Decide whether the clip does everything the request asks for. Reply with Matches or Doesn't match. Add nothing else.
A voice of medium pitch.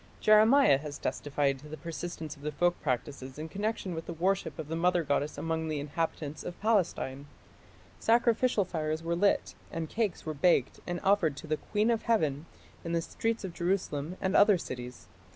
Matches